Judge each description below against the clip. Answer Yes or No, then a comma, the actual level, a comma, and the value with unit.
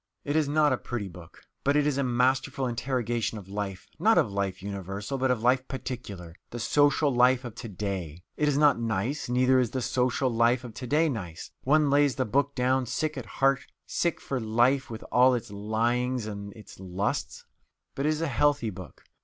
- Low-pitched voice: Yes, low, 125 Hz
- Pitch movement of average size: Yes, average, 4.3 semitones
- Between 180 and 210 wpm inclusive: Yes, fast, 205 wpm